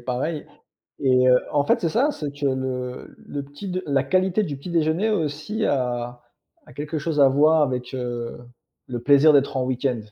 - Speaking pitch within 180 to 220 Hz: No, medium, 140 Hz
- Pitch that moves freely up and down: No, average, 3.7 semitones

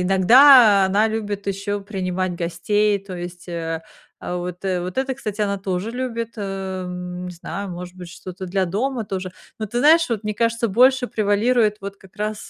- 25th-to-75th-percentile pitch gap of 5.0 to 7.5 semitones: No, average, 3.4 semitones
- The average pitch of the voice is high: Yes, high, 200 Hz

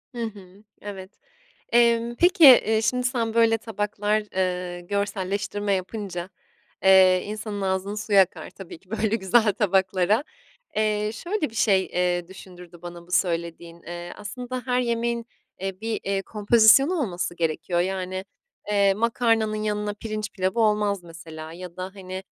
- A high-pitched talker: Yes, high, 200 Hz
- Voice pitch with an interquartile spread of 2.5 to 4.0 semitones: Yes, average, 3.4 semitones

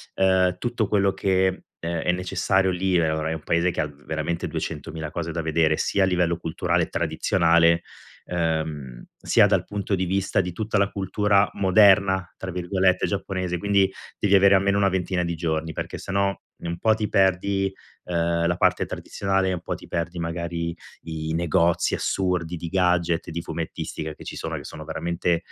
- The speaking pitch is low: Yes, very low, 90 Hz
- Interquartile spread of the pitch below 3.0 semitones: Yes, narrow, 2.4 semitones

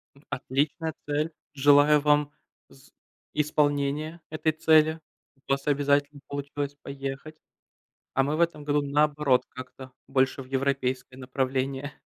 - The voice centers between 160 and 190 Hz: No, medium, 145 Hz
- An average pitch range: No, narrow, 1.8 semitones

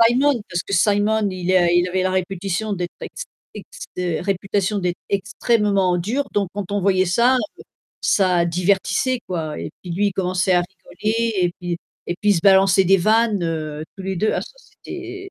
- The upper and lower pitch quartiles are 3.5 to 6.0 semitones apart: No, average, 2.7 semitones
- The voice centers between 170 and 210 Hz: Yes, high, 190 Hz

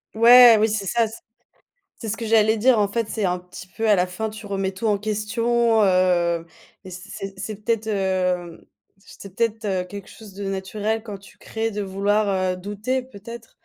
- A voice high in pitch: Yes, high, 210 Hz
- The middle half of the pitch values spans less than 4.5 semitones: Yes, average, 2.7 semitones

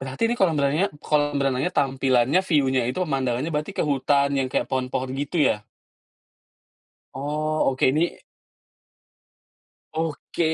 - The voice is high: No, medium, 140 Hz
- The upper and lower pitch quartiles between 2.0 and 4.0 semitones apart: Yes, average, 2.8 semitones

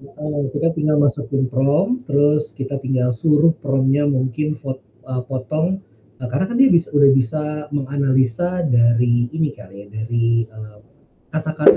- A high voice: No, medium, 140 Hz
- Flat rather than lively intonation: No, average, 3.1 semitones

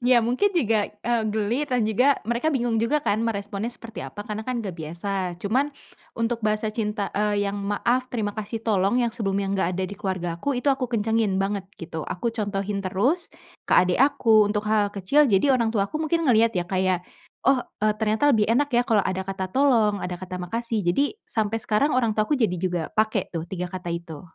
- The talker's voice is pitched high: Yes, high, 215 Hz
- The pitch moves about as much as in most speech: Yes, average, 3.6 semitones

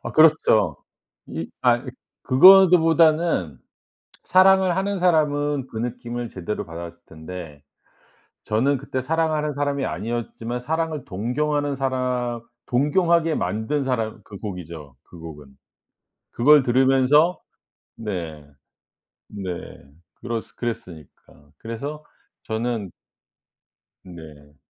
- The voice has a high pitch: No, low, 125 Hz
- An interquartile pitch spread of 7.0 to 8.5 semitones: Yes, wide, 8.0 semitones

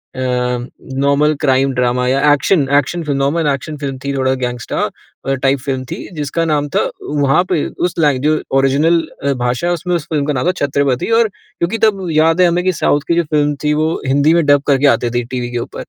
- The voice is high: No, medium, 145 Hz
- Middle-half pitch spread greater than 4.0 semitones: No, average, 3.4 semitones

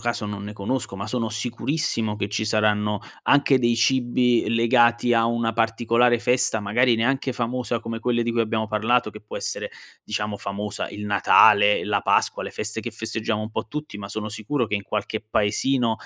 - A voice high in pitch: No, low, 115 Hz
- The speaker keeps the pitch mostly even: Yes, narrow, 2.3 semitones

